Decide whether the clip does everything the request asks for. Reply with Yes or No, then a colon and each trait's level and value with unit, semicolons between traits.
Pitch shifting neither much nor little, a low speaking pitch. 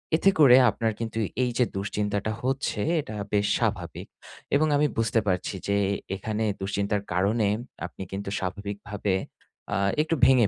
Yes: average, 3.2 semitones; low, 105 Hz